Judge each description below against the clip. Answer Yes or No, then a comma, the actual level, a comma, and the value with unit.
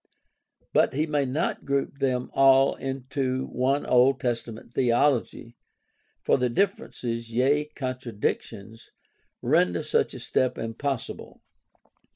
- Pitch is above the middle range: No, low, 130 Hz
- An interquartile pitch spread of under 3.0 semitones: Yes, narrow, 2.6 semitones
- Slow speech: Yes, slow, 110 wpm